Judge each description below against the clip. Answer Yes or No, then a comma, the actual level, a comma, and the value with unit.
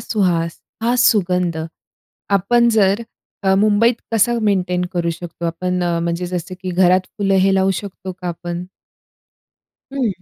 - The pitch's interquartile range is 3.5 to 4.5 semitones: No, average, 2.7 semitones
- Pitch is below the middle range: No, medium, 185 Hz